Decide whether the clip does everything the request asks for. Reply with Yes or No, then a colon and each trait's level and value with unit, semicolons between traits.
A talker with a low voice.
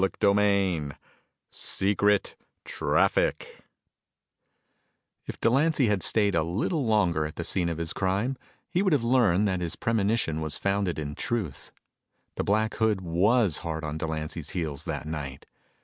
Yes: very low, 95 Hz